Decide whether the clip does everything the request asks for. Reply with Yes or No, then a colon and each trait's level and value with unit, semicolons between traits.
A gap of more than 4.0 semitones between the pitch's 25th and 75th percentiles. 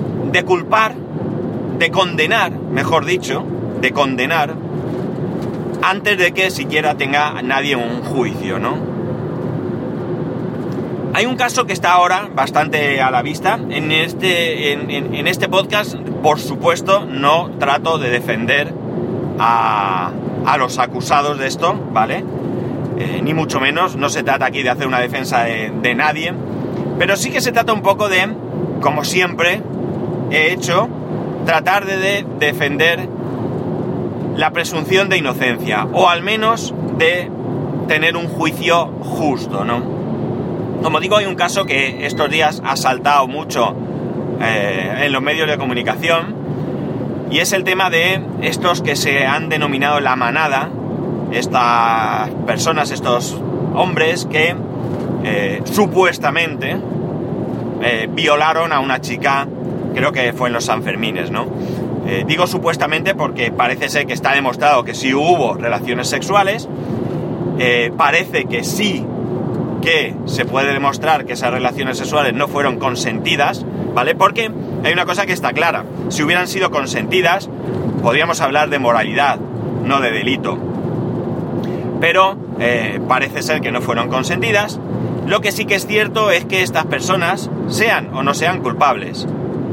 Yes: average, 5.1 semitones